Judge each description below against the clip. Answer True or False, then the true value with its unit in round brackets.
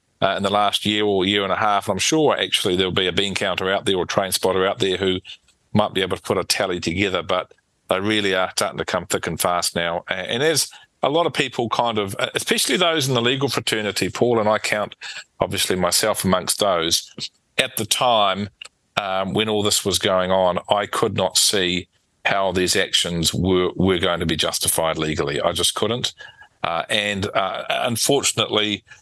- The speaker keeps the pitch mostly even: True (2.3 semitones)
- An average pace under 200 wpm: False (205 wpm)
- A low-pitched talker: True (100 Hz)